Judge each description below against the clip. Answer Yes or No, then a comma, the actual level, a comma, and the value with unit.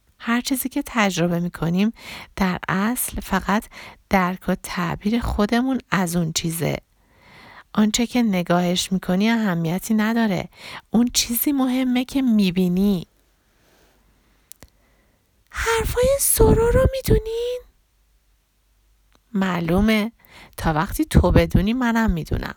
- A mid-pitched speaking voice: No, high, 210 Hz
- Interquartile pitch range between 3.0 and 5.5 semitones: Yes, average, 5.0 semitones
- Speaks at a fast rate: No, average, 110 wpm